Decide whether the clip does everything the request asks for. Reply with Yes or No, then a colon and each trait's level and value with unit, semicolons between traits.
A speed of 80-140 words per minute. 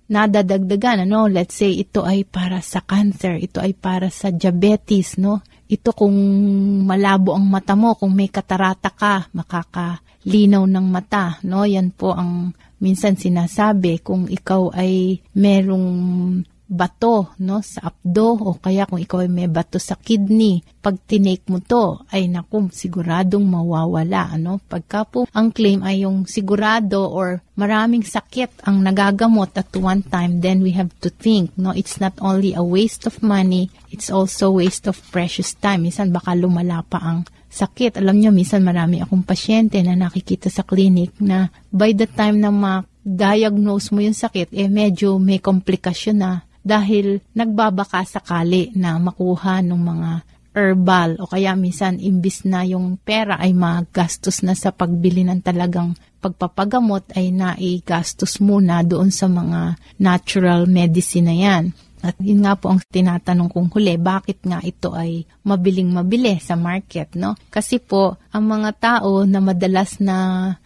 No: fast, 155 wpm